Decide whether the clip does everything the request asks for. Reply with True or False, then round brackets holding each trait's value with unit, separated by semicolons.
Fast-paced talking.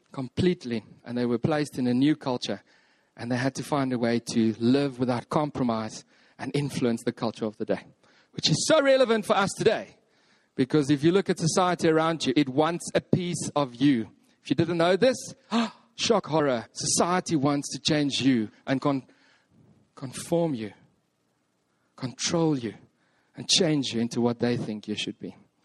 False (180 wpm)